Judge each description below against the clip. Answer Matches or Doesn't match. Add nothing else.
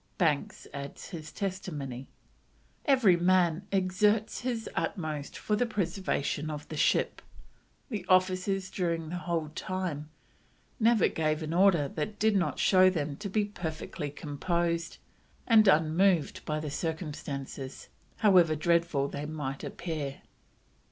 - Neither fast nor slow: Doesn't match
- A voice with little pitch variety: Doesn't match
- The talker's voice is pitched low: Doesn't match